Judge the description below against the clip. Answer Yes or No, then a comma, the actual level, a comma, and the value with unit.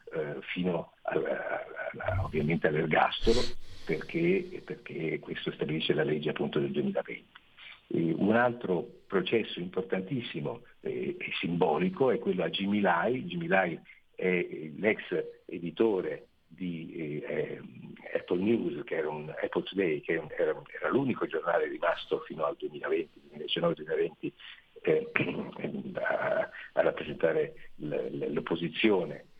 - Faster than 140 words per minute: No, slow, 115 wpm